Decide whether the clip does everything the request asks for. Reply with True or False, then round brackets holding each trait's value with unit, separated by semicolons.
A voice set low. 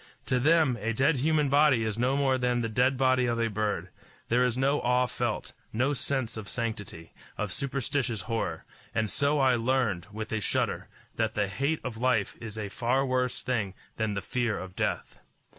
True (125 Hz)